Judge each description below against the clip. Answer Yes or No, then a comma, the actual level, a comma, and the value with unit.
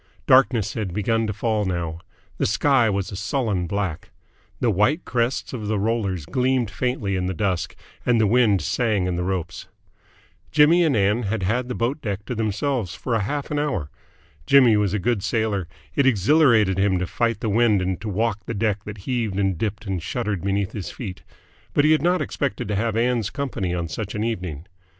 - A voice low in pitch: Yes, low, 105 Hz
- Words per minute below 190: No, average, 200 wpm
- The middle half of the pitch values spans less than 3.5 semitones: No, average, 4.0 semitones